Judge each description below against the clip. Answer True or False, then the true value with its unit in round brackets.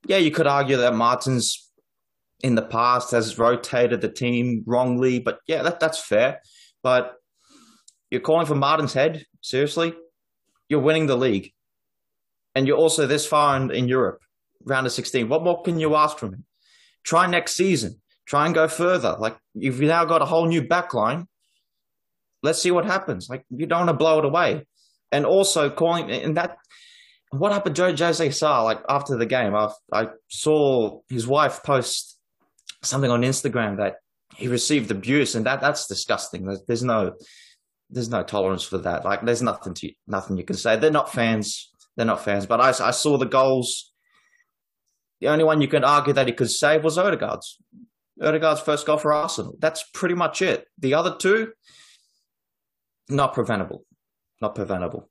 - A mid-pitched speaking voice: True (145 Hz)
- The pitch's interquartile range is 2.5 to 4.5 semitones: False (5.2 semitones)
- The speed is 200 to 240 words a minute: False (175 wpm)